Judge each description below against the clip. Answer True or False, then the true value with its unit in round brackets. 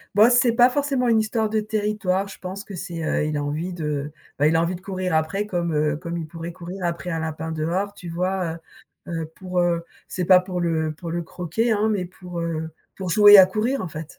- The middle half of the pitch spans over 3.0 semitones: True (3.7 semitones)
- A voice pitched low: False (180 Hz)